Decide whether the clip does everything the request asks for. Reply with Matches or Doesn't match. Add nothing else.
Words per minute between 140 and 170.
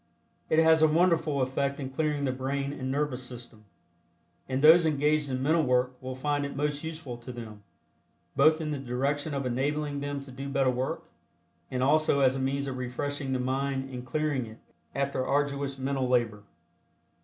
Doesn't match